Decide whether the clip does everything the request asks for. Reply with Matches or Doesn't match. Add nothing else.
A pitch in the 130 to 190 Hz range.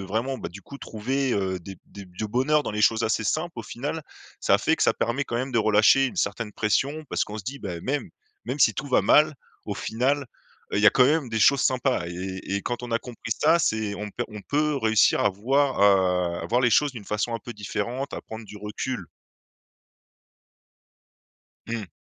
Doesn't match